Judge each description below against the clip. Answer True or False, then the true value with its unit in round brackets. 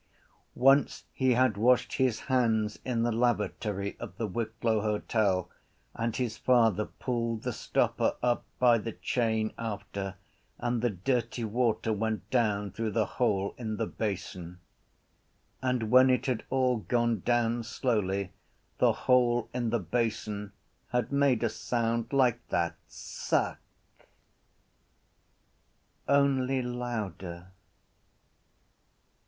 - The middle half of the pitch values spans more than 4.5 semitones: False (2.6 semitones)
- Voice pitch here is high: False (115 Hz)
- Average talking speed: False (120 wpm)